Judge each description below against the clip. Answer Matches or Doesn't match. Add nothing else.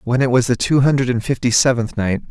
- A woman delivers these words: Doesn't match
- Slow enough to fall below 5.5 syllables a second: Doesn't match